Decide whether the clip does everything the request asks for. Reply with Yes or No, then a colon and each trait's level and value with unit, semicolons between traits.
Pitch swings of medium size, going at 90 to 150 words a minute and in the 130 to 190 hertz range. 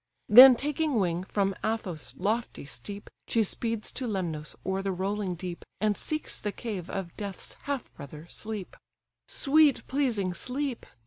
No: average, 4.9 semitones; average, 145 wpm; high, 205 Hz